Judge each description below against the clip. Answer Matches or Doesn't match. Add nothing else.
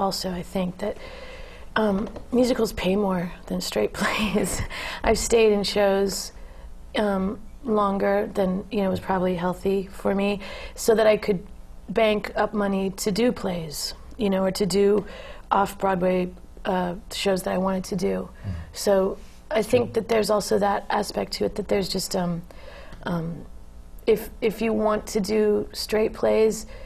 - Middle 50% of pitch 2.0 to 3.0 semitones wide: Matches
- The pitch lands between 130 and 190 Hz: Doesn't match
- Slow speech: Doesn't match